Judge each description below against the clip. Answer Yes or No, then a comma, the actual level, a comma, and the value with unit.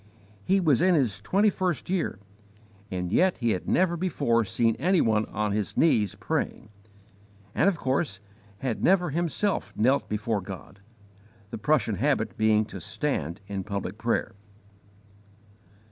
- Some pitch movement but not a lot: No, wide, 8.1 semitones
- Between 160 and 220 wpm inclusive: No, average, 145 wpm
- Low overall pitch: Yes, low, 115 Hz